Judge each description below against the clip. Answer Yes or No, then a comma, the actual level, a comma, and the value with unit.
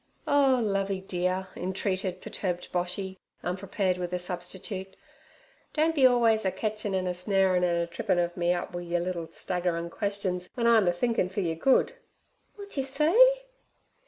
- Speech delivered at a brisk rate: No, average, 165 wpm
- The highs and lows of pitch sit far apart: No, average, 3.6 semitones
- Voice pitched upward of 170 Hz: Yes, high, 190 Hz